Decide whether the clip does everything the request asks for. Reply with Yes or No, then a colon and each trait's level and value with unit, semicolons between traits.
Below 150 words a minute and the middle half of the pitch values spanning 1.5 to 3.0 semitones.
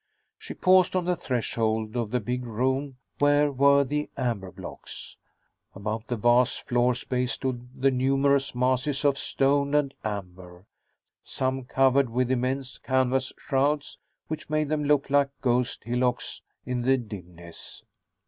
Yes: average, 140 wpm; narrow, 2.6 semitones